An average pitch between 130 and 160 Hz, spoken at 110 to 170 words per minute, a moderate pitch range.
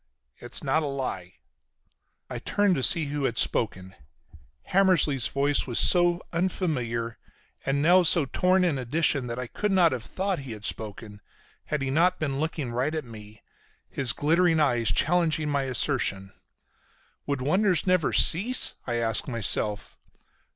No: medium, 140 Hz; average, 150 wpm; wide, 6.2 semitones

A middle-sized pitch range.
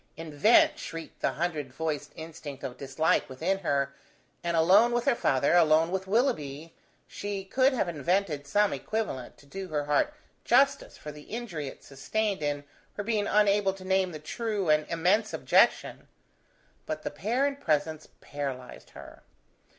No: wide, 5.8 semitones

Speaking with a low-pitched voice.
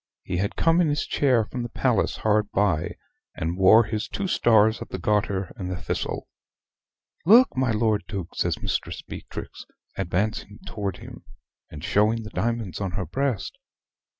Yes: low, 105 Hz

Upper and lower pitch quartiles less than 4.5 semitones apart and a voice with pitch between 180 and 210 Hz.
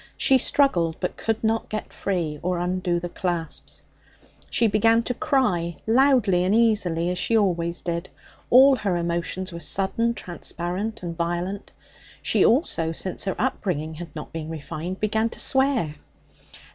No: average, 4.8 semitones; medium, 185 Hz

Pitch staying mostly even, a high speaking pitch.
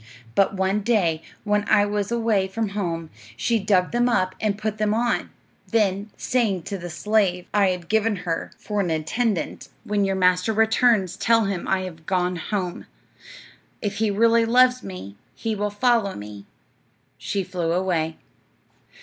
No: average, 3.3 semitones; high, 200 Hz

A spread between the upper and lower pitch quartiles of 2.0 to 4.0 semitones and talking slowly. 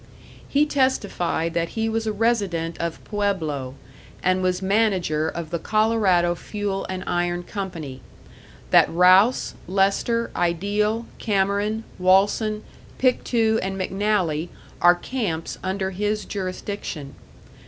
Yes: average, 3.5 semitones; slow, 110 wpm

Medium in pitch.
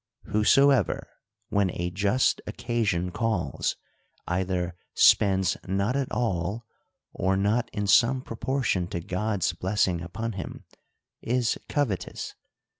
No: low, 100 Hz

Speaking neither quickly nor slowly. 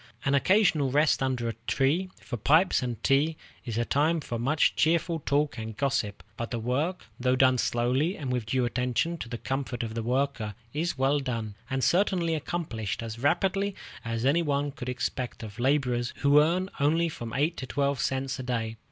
Yes: average, 190 wpm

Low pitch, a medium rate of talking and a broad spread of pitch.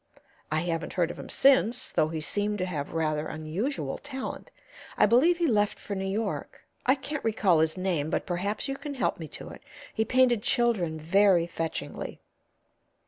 No: high, 195 Hz; average, 180 wpm; wide, 6.7 semitones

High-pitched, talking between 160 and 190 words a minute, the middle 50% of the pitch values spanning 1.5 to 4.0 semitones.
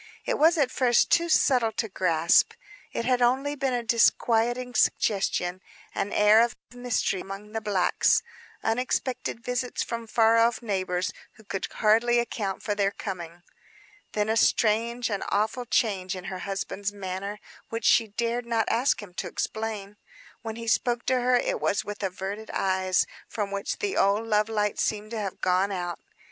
Yes: high, 220 Hz; average, 170 wpm; average, 3.3 semitones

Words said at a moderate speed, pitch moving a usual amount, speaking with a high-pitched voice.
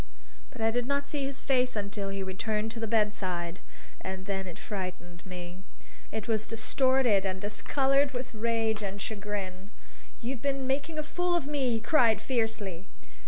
Yes: average, 165 wpm; average, 5.0 semitones; high, 220 Hz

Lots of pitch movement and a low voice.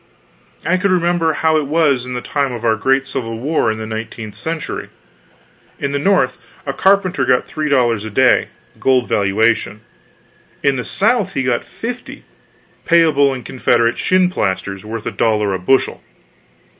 Yes: wide, 6.0 semitones; low, 130 Hz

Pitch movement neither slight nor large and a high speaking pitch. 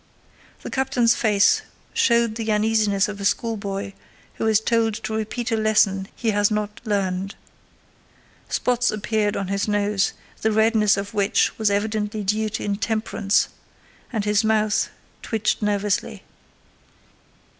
No: narrow, 1.6 semitones; high, 210 Hz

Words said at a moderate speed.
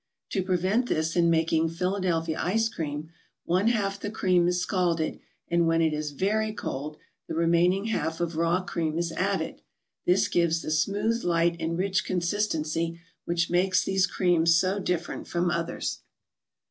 Yes: average, 160 wpm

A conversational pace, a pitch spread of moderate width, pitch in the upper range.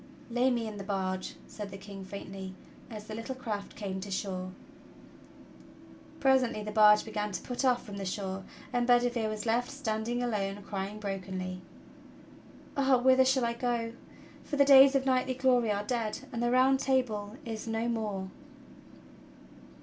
Yes: average, 165 wpm; average, 3.6 semitones; high, 220 Hz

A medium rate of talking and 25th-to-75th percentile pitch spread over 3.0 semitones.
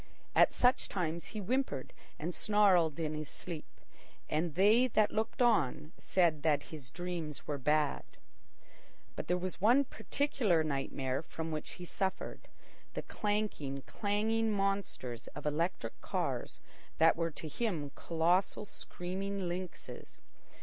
No: slow, 130 wpm; average, 5.0 semitones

